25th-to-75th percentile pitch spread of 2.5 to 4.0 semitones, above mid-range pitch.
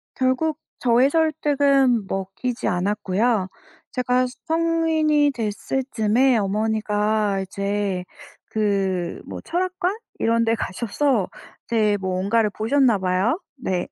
No: average, 5.3 semitones; high, 225 Hz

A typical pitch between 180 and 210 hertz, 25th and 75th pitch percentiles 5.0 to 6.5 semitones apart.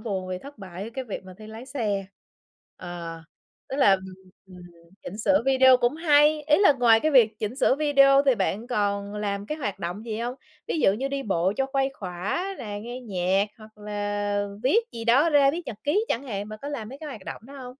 No: high, 225 Hz; average, 5.3 semitones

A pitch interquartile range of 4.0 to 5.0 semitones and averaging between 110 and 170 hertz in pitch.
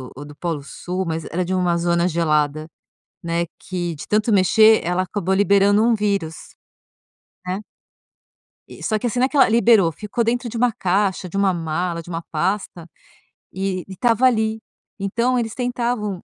No: average, 4.3 semitones; high, 190 Hz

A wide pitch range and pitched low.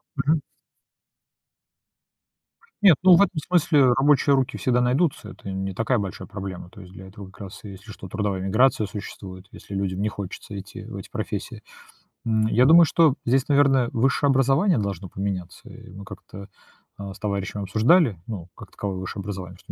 Yes: wide, 5.7 semitones; low, 105 Hz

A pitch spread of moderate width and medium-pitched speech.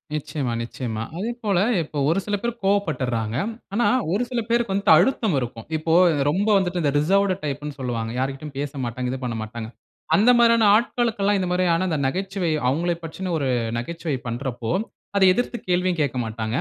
No: wide, 7.5 semitones; medium, 160 Hz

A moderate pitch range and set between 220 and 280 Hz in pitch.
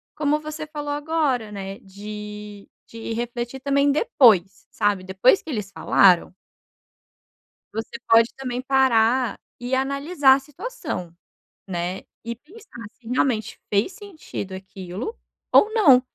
No: wide, 5.7 semitones; high, 245 Hz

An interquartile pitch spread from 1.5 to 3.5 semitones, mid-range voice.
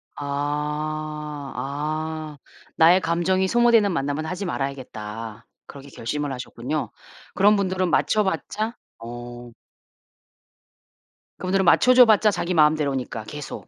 No: wide, 5.4 semitones; medium, 155 Hz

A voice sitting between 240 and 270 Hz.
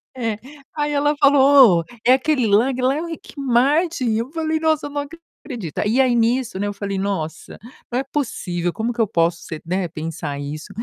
Yes: high, 245 Hz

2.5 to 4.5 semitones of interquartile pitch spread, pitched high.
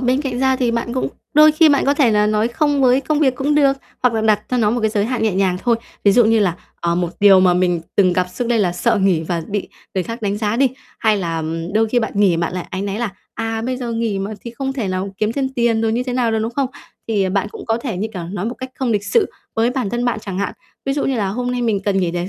Yes: average, 4.2 semitones; high, 225 Hz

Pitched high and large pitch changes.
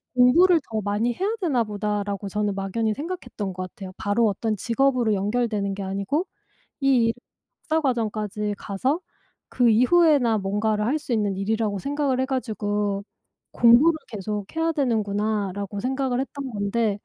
No: high, 220 Hz; average, 4.4 semitones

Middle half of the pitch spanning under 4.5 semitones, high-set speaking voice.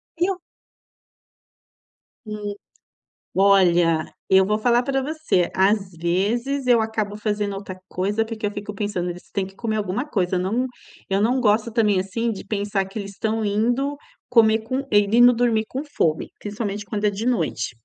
Yes: average, 3.2 semitones; high, 210 Hz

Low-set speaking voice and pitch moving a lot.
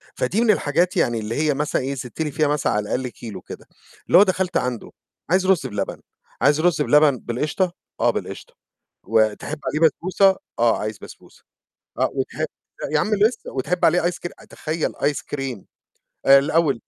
No: medium, 150 Hz; wide, 5.7 semitones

